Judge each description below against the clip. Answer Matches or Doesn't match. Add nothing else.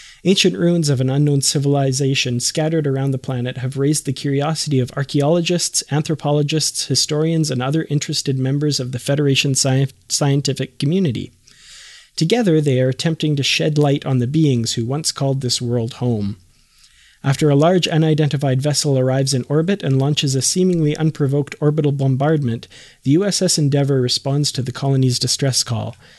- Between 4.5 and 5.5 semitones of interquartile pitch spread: Doesn't match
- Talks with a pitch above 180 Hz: Doesn't match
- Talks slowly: Doesn't match